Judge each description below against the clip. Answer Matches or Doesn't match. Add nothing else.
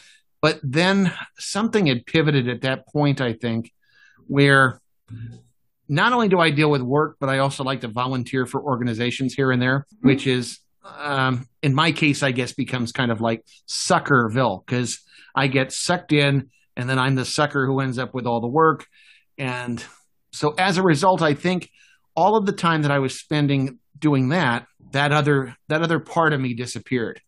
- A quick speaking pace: Doesn't match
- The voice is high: Doesn't match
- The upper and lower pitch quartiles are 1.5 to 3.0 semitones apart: Doesn't match